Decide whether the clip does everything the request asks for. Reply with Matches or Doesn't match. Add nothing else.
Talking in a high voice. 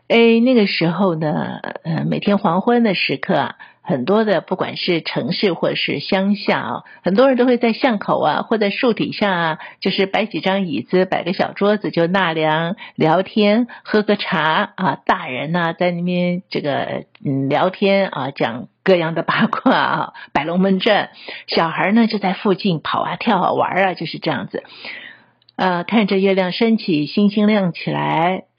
Matches